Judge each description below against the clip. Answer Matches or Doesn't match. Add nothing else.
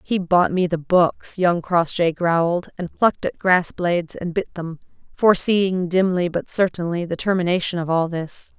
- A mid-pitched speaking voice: Matches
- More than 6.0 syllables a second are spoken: Doesn't match